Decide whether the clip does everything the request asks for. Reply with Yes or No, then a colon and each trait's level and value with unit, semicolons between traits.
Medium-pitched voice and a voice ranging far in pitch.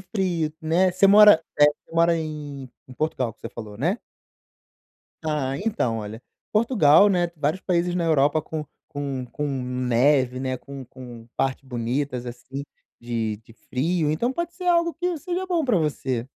Yes: medium, 150 Hz; wide, 6.2 semitones